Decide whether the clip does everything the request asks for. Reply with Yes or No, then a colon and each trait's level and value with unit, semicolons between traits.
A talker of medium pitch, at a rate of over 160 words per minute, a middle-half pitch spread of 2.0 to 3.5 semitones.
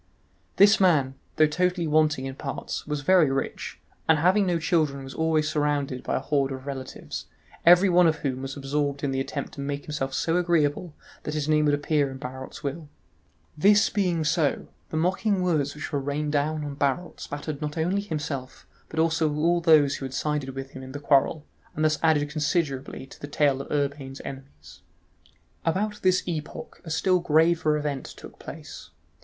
Yes: medium, 150 Hz; average, 185 wpm; average, 2.8 semitones